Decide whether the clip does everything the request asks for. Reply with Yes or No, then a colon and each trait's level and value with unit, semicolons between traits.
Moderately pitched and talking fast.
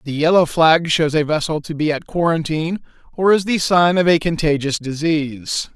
No: medium, 160 Hz; average, 190 wpm